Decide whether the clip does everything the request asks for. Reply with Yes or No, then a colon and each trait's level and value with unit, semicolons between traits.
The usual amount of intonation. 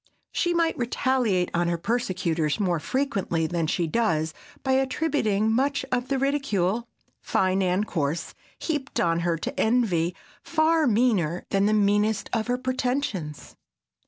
No: wide, 7.0 semitones